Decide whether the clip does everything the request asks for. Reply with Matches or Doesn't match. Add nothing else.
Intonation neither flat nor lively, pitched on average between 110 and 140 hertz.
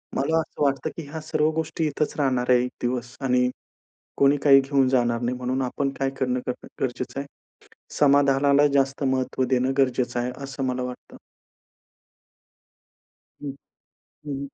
Doesn't match